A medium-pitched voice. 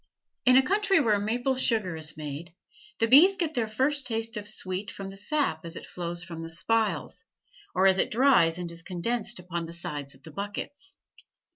No: high, 200 Hz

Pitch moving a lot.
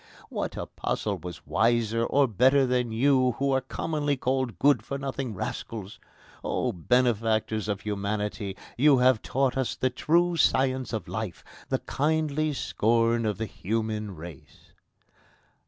No: average, 3.8 semitones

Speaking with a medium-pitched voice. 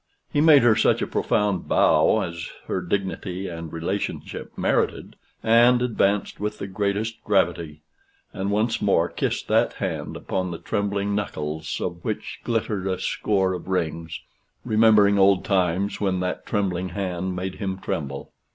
No: very low, 95 Hz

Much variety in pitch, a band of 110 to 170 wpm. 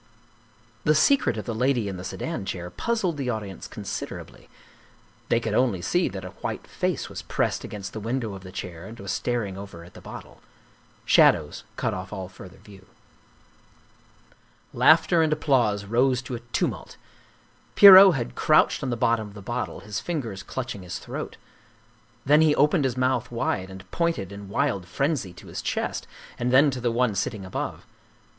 No: wide, 5.9 semitones; average, 180 wpm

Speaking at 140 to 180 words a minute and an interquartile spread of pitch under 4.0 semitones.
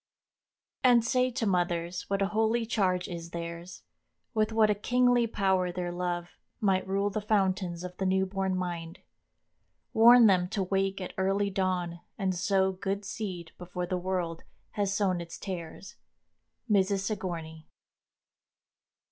Yes: average, 150 wpm; narrow, 2.4 semitones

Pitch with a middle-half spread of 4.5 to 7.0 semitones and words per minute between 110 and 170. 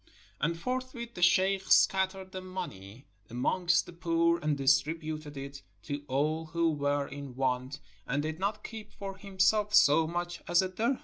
Yes: average, 4.8 semitones; average, 165 wpm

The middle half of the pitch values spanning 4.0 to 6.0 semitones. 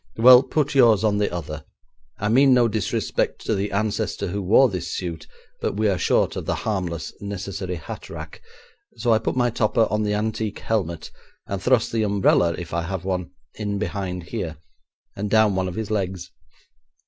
No: average, 3.3 semitones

